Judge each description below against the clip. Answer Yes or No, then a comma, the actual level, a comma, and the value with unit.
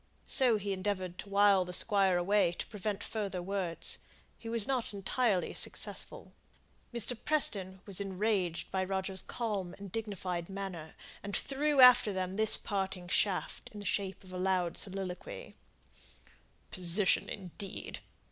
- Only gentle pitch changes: Yes, narrow, 2.3 semitones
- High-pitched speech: Yes, high, 195 Hz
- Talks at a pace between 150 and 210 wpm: No, average, 140 wpm